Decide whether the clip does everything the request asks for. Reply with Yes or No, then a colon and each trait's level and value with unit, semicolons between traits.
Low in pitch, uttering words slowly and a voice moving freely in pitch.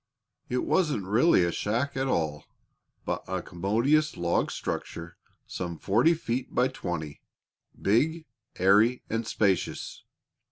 Yes: low, 110 Hz; slow, 120 wpm; wide, 6.9 semitones